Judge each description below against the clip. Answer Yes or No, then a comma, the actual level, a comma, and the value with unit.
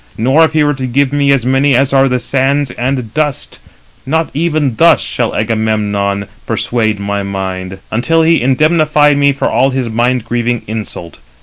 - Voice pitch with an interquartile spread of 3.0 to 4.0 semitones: No, average, 4.5 semitones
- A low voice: Yes, low, 130 Hz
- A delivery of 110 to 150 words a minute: No, average, 180 wpm